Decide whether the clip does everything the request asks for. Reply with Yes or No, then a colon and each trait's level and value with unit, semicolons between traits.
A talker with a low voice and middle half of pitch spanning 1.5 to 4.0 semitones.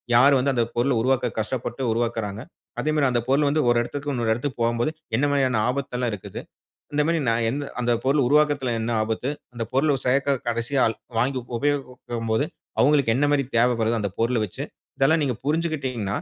Yes: low, 125 Hz; average, 3.4 semitones